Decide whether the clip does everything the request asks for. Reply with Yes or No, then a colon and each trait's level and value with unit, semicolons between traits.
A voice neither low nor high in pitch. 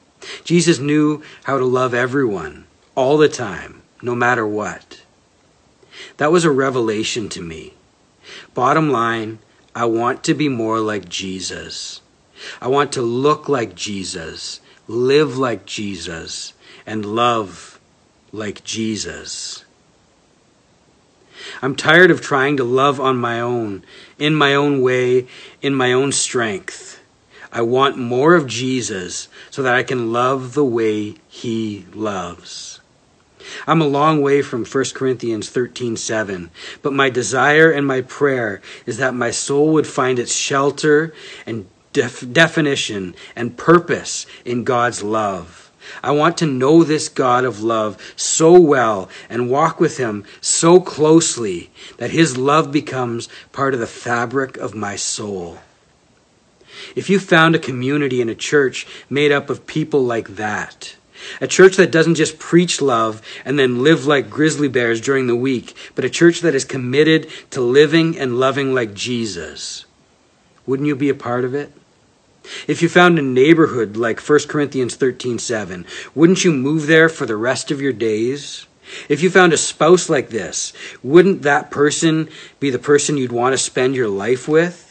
No: low, 130 Hz